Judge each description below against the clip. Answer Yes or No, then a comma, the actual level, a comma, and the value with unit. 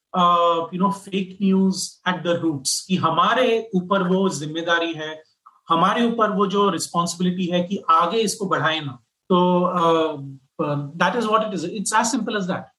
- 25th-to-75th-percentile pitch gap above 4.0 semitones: No, average, 3.2 semitones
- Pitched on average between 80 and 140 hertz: No, medium, 180 Hz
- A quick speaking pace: No, average, 170 wpm